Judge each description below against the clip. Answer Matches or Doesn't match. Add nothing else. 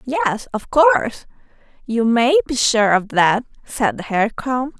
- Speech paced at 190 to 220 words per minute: Doesn't match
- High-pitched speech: Matches